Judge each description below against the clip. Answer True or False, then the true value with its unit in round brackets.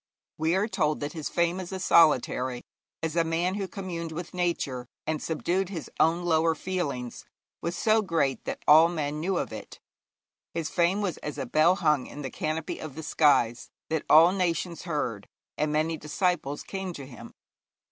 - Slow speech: False (185 wpm)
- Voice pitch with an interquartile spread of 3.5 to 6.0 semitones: False (2.8 semitones)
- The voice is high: False (165 Hz)